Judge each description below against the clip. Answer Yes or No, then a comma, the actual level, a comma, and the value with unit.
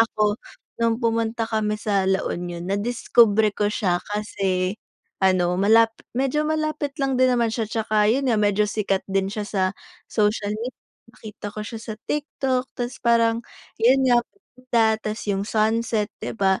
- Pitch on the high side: Yes, high, 220 Hz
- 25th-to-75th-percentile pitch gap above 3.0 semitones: No, narrow, 2.5 semitones